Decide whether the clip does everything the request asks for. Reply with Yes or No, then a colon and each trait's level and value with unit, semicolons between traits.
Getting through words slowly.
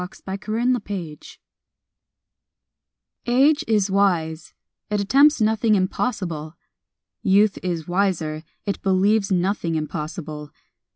Yes: slow, 95 wpm